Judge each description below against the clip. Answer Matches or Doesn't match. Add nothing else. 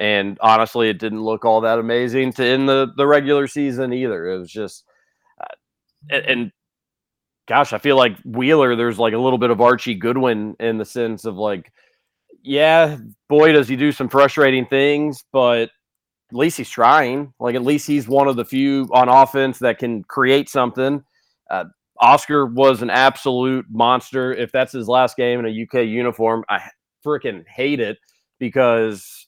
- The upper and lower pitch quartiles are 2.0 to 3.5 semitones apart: Matches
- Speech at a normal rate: Matches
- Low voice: Matches